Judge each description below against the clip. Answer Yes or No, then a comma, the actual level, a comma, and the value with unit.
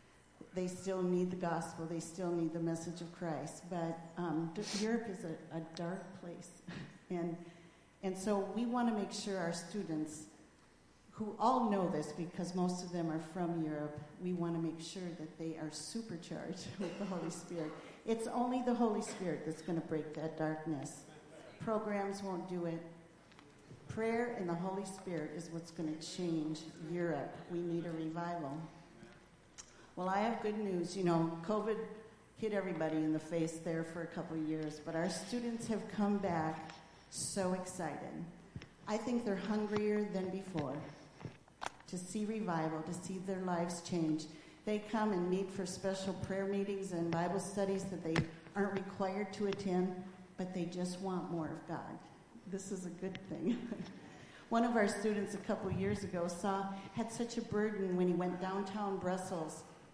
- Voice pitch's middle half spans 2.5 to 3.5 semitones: Yes, average, 3.2 semitones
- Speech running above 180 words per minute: No, average, 175 wpm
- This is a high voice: No, medium, 180 Hz